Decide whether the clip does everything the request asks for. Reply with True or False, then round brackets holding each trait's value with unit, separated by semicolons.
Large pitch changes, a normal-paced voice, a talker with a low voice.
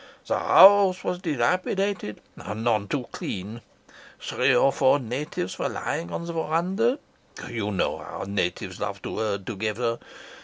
True (9.0 semitones; 145 wpm; 120 Hz)